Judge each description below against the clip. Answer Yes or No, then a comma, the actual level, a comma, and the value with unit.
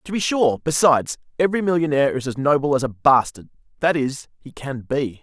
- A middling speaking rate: Yes, average, 185 wpm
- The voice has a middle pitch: Yes, medium, 145 Hz